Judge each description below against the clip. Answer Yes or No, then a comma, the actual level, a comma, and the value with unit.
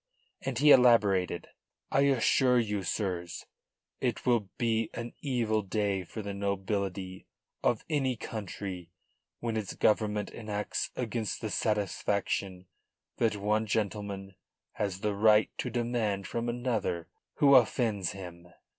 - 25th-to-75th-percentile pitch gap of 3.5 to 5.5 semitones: No, average, 3.1 semitones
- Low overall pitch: Yes, low, 105 Hz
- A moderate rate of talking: No, slow, 125 wpm